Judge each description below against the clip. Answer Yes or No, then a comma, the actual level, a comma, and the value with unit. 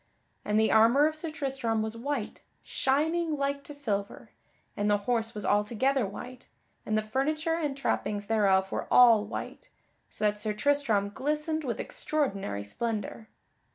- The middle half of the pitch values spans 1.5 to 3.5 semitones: No, wide, 5.4 semitones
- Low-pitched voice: No, high, 235 Hz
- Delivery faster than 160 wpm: No, average, 155 wpm